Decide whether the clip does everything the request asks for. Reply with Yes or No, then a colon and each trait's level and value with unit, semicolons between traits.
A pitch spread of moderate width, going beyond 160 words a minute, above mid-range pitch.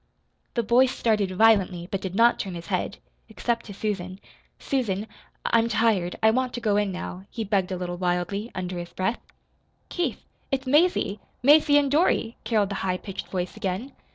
Yes: average, 4.3 semitones; average, 180 wpm; high, 210 Hz